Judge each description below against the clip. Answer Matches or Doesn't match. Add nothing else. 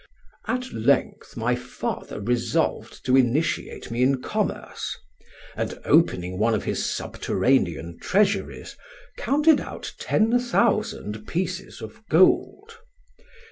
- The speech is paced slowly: Matches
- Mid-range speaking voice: Matches